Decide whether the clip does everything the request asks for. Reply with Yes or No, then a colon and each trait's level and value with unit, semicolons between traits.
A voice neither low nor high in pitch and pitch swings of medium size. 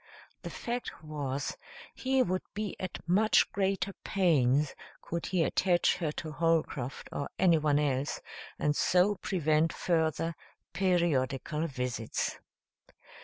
Yes: medium, 165 Hz; average, 4.0 semitones